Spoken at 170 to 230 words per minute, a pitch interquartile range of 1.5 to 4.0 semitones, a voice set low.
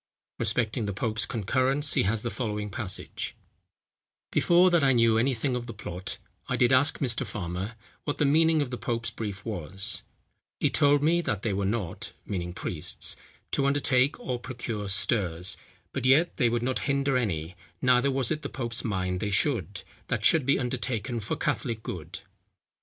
No: average, 175 wpm; average, 4.9 semitones; low, 115 Hz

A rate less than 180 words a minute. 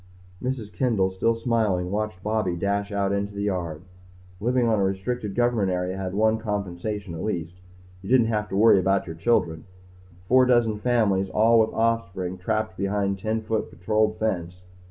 Yes: average, 170 wpm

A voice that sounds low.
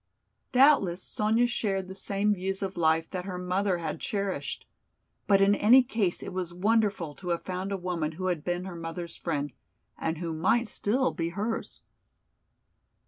No: medium, 185 Hz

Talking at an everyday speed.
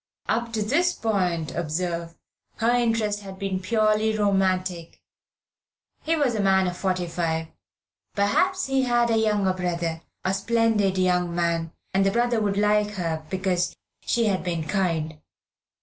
Yes: average, 150 wpm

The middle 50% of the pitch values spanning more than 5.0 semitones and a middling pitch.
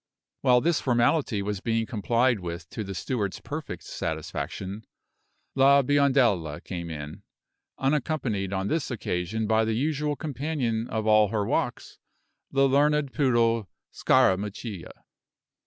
No: wide, 5.4 semitones; low, 115 Hz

